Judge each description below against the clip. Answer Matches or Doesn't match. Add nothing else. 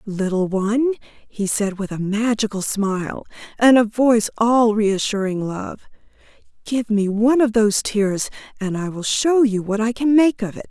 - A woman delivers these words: Matches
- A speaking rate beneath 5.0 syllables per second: Matches